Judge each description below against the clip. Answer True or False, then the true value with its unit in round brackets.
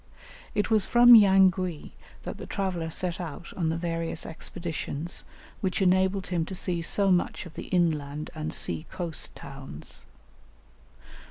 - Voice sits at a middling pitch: True (175 Hz)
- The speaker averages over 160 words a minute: False (145 wpm)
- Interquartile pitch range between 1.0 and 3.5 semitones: True (2.7 semitones)